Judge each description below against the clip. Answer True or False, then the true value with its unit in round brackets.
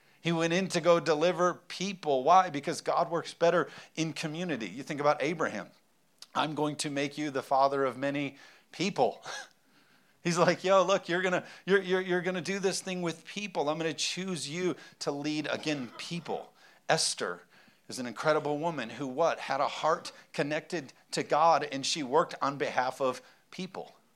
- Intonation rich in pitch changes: False (3.5 semitones)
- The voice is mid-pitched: True (160 Hz)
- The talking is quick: False (175 wpm)